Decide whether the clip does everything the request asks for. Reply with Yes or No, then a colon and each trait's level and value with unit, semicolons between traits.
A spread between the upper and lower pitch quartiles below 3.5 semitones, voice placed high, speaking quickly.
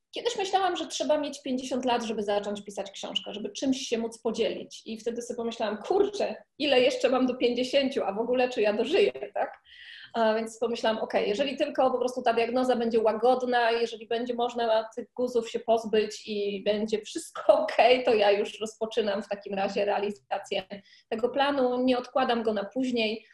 Yes: average, 2.9 semitones; high, 235 Hz; fast, 185 wpm